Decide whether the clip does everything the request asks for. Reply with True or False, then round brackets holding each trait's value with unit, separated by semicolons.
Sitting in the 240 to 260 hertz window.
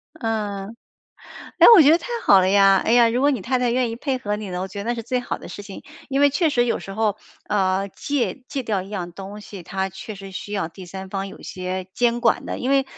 False (210 Hz)